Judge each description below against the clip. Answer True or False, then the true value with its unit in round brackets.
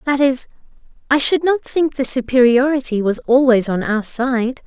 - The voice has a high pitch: True (260 Hz)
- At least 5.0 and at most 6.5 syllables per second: False (4.6 syllables/s)